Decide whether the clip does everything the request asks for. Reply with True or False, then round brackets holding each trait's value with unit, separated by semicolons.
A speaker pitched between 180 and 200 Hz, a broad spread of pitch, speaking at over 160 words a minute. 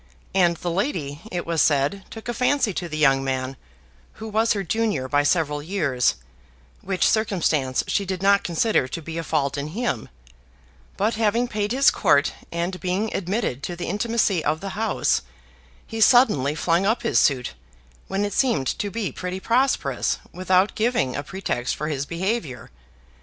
True (185 Hz; 6.4 semitones; 170 wpm)